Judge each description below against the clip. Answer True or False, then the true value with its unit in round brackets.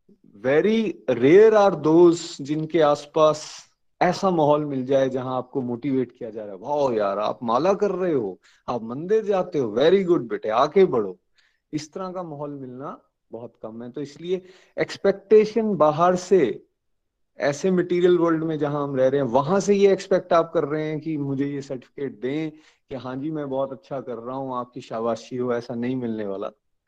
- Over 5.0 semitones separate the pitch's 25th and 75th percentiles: True (5.5 semitones)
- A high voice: False (155 Hz)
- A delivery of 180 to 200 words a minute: True (190 wpm)